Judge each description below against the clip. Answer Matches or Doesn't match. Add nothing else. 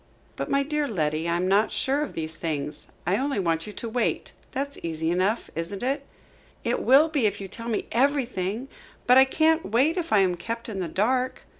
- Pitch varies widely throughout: Matches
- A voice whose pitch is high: Matches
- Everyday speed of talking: Doesn't match